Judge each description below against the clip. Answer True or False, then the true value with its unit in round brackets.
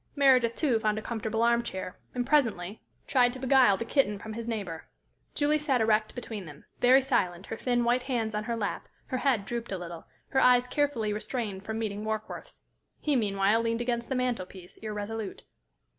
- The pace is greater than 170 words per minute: True (190 wpm)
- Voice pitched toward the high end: True (230 Hz)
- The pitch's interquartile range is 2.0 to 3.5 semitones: True (3.1 semitones)